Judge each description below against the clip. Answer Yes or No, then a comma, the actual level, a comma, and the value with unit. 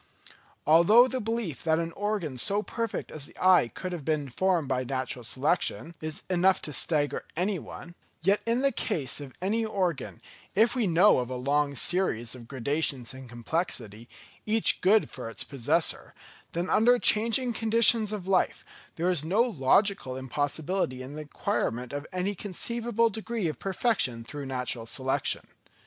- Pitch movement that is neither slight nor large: No, wide, 7.7 semitones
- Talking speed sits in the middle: Yes, average, 160 wpm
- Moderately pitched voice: Yes, medium, 170 Hz